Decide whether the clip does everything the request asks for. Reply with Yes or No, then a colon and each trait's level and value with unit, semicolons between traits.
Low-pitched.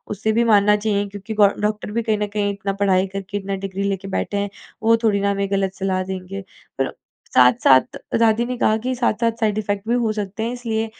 No: high, 205 Hz